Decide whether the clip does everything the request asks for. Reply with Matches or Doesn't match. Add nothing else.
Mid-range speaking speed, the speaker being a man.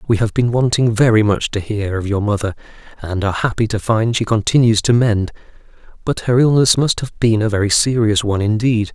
Doesn't match